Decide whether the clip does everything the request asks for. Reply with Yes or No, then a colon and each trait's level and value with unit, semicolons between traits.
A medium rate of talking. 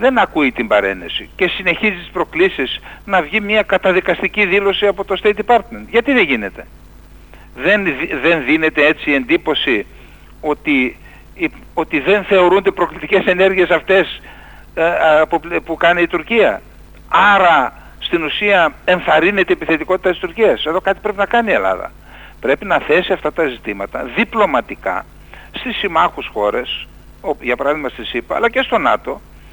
Yes: average, 150 wpm